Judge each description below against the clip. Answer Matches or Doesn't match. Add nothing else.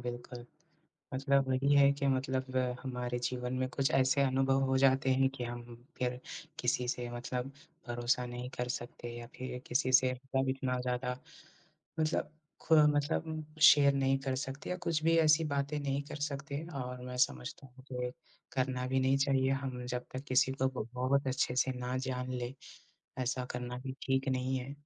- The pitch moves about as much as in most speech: Doesn't match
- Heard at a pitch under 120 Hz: Doesn't match